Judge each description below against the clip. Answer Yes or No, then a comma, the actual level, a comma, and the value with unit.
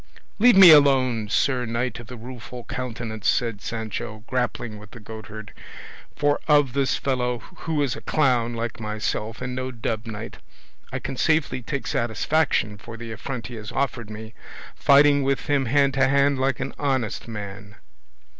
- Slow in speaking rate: No, average, 165 wpm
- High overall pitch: No, low, 120 Hz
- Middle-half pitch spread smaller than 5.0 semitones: Yes, average, 3.6 semitones